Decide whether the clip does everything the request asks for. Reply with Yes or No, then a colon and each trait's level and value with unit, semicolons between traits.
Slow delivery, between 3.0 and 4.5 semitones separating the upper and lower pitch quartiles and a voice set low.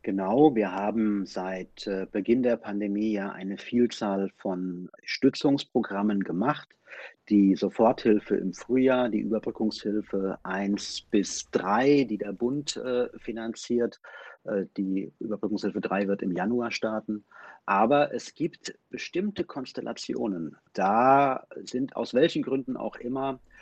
Yes: slow, 115 wpm; average, 4.1 semitones; low, 110 Hz